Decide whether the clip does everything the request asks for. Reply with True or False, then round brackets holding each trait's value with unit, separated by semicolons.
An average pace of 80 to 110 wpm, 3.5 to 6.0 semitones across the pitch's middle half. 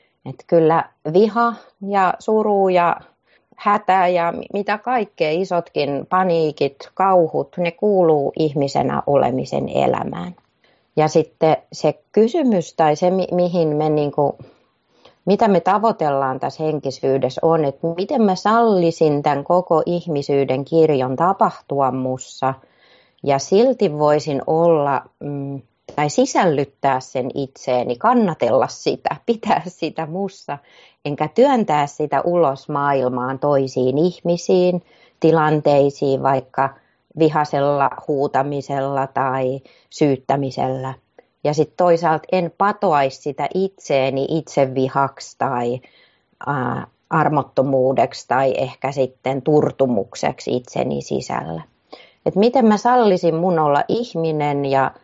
True (105 wpm; 4.7 semitones)